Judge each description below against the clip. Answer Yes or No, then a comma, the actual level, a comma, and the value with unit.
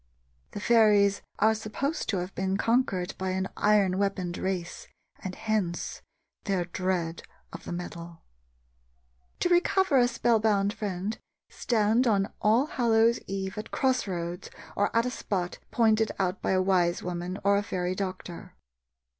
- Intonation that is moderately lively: Yes, average, 3.3 semitones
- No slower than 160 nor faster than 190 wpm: No, average, 145 wpm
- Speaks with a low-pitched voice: No, high, 200 Hz